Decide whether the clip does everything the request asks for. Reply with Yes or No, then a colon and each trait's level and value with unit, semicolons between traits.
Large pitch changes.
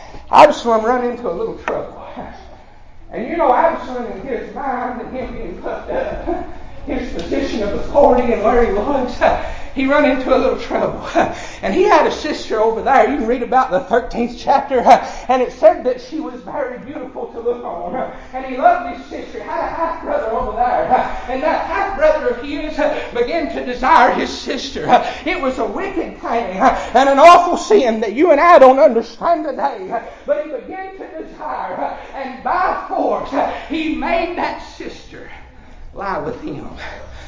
No: average, 4.9 semitones